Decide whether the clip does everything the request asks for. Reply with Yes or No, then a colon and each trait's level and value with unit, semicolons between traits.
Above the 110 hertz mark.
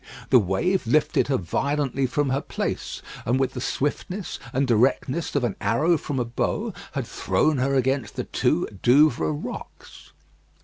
Yes: low, 135 Hz